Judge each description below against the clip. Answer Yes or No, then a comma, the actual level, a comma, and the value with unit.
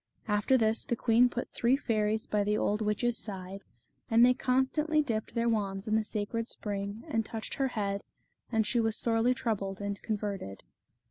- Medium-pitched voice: No, high, 220 Hz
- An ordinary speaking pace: Yes, average, 180 wpm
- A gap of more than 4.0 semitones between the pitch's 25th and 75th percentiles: No, narrow, 2.5 semitones